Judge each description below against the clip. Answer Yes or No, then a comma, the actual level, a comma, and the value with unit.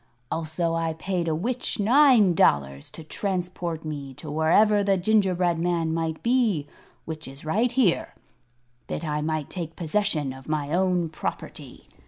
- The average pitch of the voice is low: No, medium, 165 Hz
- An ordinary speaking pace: Yes, average, 150 wpm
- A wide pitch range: No, average, 3.9 semitones